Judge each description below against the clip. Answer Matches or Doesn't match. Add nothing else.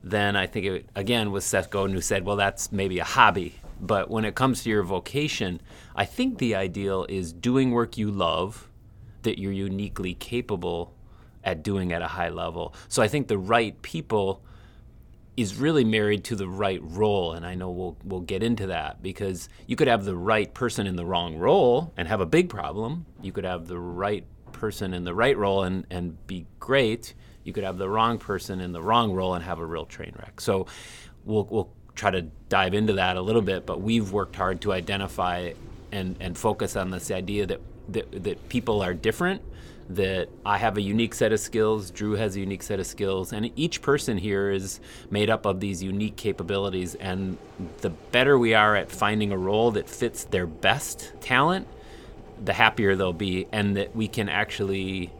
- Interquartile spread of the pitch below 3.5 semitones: Matches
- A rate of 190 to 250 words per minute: Matches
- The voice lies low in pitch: Matches